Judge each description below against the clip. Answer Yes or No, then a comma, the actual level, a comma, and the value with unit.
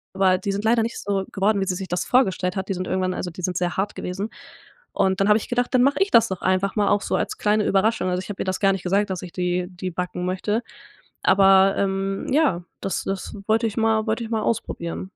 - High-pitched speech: Yes, high, 195 Hz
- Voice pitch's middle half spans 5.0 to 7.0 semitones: No, narrow, 2.6 semitones